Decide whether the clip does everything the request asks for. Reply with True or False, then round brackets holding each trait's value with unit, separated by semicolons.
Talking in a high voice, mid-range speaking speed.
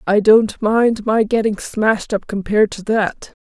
True (215 Hz; 175 wpm)